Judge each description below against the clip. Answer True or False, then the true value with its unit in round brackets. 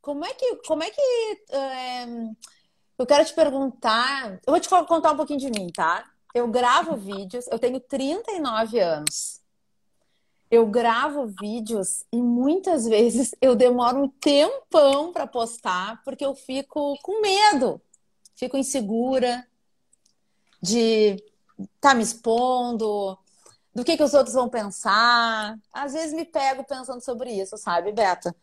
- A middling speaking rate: True (140 wpm)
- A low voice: False (250 Hz)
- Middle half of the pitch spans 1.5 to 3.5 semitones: False (4.6 semitones)